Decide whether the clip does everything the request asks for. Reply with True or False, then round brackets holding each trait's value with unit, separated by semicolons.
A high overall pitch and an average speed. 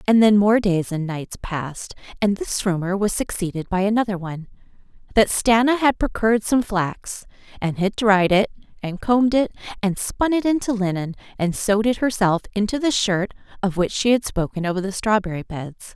True (205 Hz; 180 wpm)